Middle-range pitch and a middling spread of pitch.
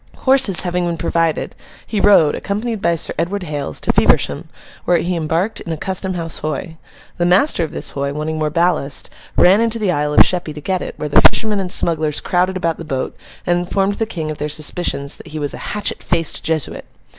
Yes: medium, 170 Hz; average, 3.6 semitones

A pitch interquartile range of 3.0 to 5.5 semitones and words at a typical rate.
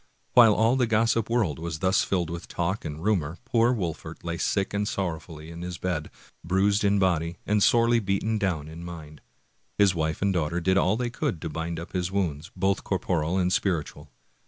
Yes: average, 3.6 semitones; average, 195 wpm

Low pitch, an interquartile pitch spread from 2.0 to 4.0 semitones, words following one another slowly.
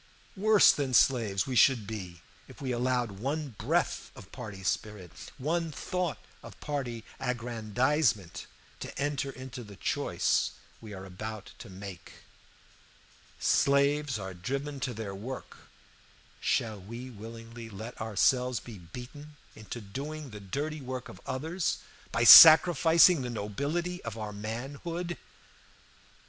No: low, 125 Hz; average, 5.1 semitones; slow, 130 wpm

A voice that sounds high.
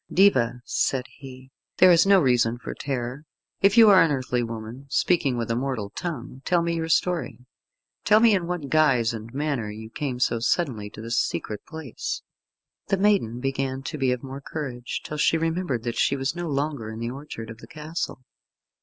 No: low, 135 Hz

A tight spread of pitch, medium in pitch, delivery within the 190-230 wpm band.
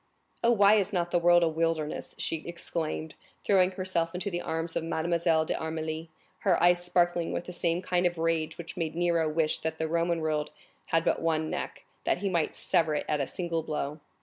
Yes: narrow, 1.7 semitones; medium, 165 Hz; fast, 205 wpm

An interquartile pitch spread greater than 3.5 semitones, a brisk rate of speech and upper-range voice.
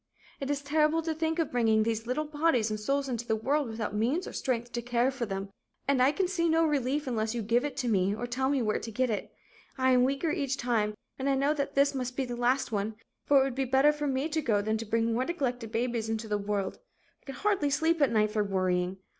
Yes: average, 4.2 semitones; fast, 260 wpm; very high, 250 Hz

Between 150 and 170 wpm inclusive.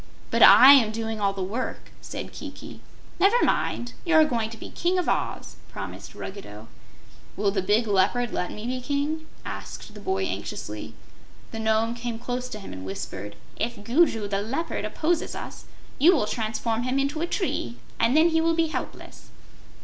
No: average, 180 wpm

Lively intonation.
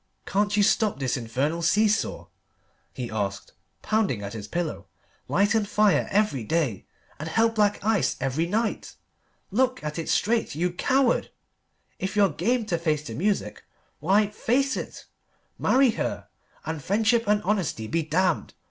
Yes: wide, 6.0 semitones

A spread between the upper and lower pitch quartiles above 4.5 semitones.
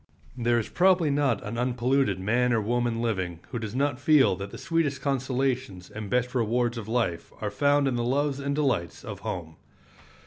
No: average, 4.1 semitones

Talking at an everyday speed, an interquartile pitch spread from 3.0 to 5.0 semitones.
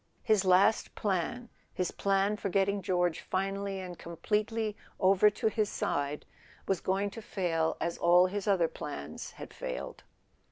No: average, 155 wpm; narrow, 2.6 semitones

